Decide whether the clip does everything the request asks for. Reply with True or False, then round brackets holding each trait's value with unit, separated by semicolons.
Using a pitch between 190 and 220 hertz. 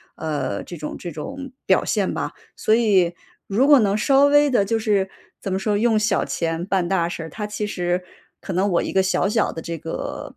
True (195 Hz)